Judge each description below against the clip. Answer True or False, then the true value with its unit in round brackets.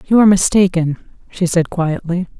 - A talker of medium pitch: True (180 Hz)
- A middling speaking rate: True (150 wpm)